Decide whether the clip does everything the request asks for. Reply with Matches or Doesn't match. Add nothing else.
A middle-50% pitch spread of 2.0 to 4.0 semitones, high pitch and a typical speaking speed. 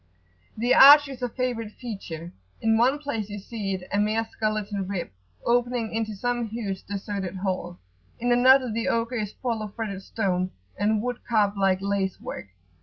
Matches